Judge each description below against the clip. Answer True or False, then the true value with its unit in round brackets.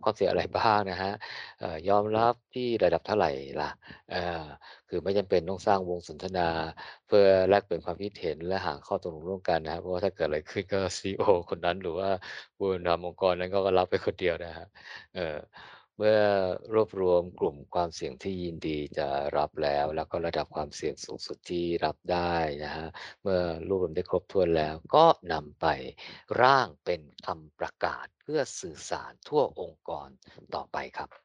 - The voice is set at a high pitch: False (90 Hz)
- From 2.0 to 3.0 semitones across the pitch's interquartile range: True (2.6 semitones)